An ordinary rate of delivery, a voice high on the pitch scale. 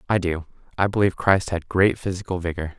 No: average, 170 wpm; very low, 90 Hz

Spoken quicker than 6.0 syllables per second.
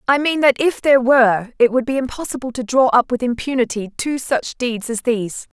No: 5.6 syllables/s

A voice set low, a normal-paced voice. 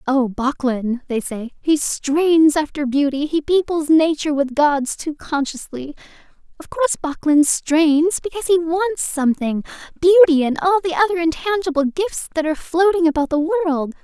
No: very high, 310 Hz; average, 150 wpm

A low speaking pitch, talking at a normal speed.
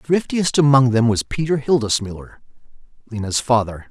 No: low, 125 Hz; slow, 125 wpm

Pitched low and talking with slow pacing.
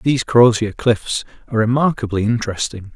Yes: low, 115 Hz; slow, 120 wpm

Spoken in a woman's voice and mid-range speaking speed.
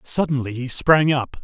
No: male; average, 170 wpm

